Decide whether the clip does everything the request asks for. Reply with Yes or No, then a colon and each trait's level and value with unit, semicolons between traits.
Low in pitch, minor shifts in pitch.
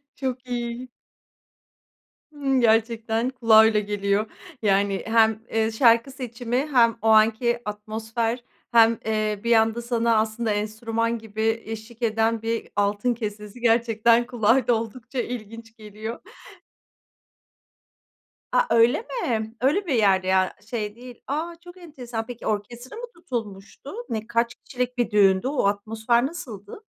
No: high, 230 Hz; narrow, 2.0 semitones